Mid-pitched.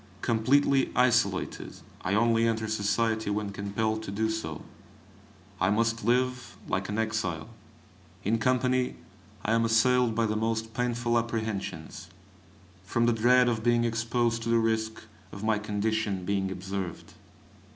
No: low, 110 Hz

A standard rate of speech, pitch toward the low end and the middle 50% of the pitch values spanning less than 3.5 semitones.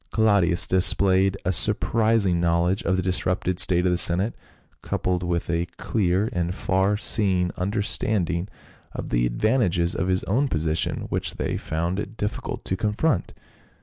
Yes: average, 150 wpm; very low, 95 Hz; average, 2.8 semitones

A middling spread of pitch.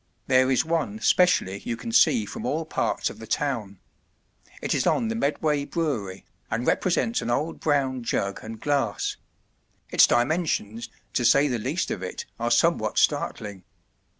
No: wide, 6.4 semitones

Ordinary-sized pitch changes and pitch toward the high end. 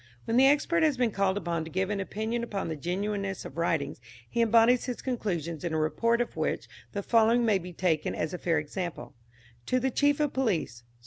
No: wide, 5.7 semitones; high, 200 Hz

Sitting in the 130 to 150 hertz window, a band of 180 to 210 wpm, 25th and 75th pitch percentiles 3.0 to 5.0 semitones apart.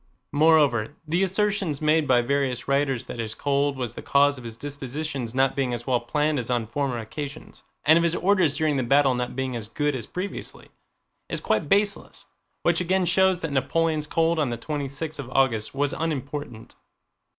Yes: medium, 140 Hz; average, 190 wpm; average, 4.0 semitones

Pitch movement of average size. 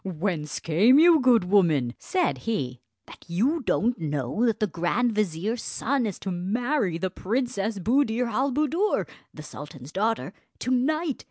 No: wide, 6.5 semitones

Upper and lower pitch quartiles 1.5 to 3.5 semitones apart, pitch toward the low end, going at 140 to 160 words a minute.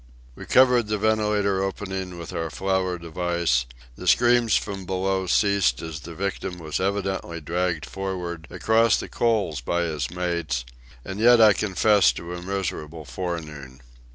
Yes: average, 3.2 semitones; very low, 90 Hz; average, 150 wpm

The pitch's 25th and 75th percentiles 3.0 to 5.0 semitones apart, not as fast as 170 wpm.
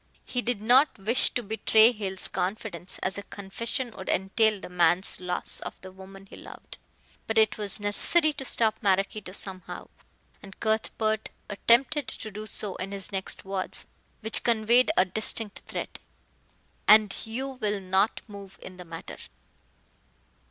No: narrow, 2.6 semitones; average, 150 wpm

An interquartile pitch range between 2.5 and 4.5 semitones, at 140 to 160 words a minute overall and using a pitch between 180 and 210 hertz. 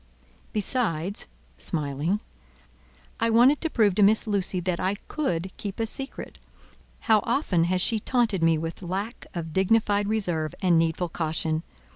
No: average, 4.9 semitones; average, 145 wpm; high, 190 Hz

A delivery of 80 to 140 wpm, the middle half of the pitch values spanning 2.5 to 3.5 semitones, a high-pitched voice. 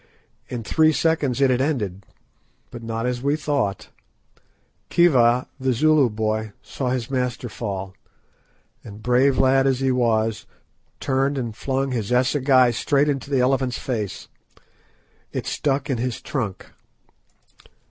No: slow, 135 wpm; average, 3.0 semitones; low, 125 Hz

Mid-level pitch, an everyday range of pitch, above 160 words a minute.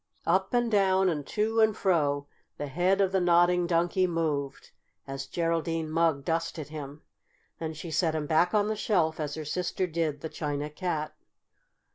Yes: medium, 165 Hz; average, 3.4 semitones; average, 170 wpm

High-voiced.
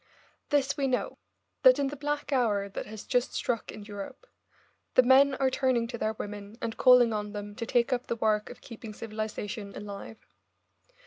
Yes: high, 230 Hz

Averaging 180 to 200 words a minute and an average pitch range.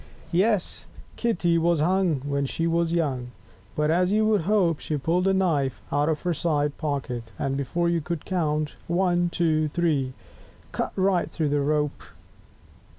No: average, 170 wpm; average, 3.2 semitones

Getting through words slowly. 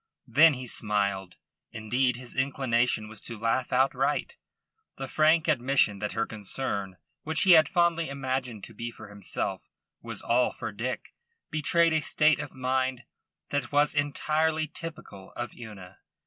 No: average, 150 wpm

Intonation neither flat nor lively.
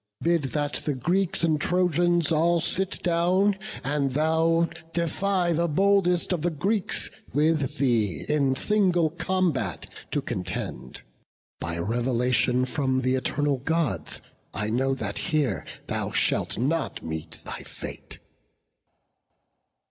Yes: average, 5.0 semitones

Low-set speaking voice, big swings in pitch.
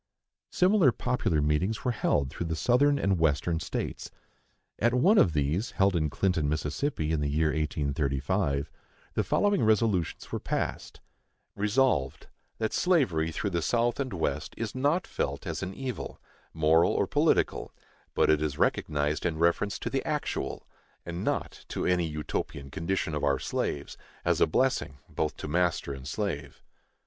Yes: very low, 85 Hz; wide, 6.8 semitones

